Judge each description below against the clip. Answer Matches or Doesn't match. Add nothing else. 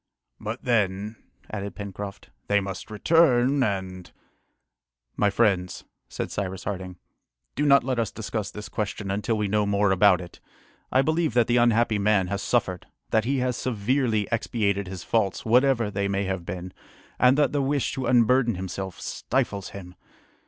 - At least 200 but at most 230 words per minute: Doesn't match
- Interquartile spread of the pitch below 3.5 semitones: Doesn't match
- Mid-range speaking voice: Doesn't match